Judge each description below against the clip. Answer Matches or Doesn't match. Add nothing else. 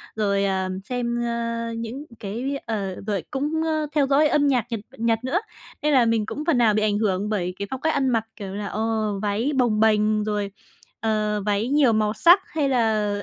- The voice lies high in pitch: Matches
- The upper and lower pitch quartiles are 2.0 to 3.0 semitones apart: Doesn't match